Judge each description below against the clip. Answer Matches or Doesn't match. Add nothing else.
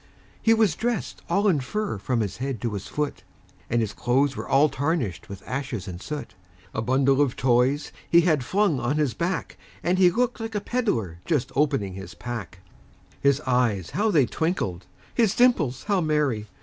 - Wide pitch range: Matches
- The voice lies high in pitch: Doesn't match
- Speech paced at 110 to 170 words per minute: Doesn't match